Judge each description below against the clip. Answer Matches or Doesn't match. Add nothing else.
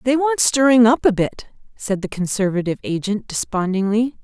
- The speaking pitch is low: Doesn't match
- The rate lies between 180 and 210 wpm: Doesn't match